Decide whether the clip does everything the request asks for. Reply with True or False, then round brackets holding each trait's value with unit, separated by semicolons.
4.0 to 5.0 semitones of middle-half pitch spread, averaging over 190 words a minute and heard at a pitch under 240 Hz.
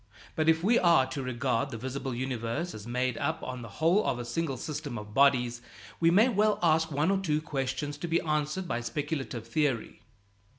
True (4.7 semitones; 200 wpm; 140 Hz)